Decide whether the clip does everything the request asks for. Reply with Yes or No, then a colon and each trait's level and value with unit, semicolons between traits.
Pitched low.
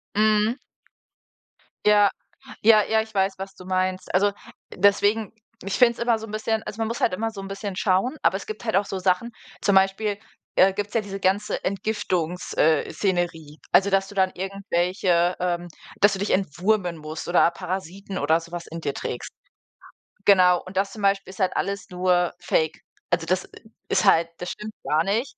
No: high, 195 Hz